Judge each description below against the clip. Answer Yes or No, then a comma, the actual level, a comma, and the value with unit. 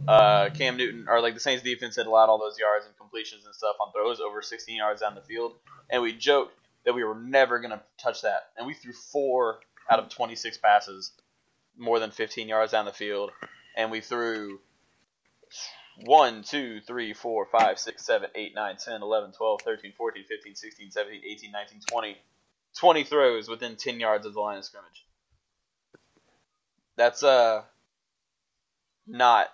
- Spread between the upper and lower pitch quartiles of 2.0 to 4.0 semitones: Yes, average, 3.0 semitones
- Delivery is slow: No, average, 175 wpm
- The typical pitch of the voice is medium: No, low, 115 Hz